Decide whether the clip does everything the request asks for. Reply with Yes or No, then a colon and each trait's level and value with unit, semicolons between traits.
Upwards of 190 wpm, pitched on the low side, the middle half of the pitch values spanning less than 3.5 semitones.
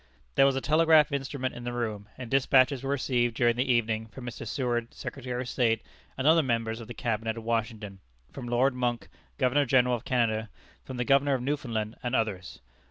Yes: average, 200 wpm; low, 120 Hz; narrow, 2.6 semitones